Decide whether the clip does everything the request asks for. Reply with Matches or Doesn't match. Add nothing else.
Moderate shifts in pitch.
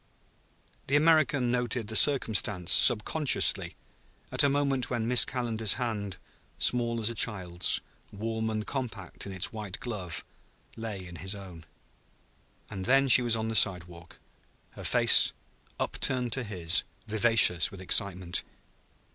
Matches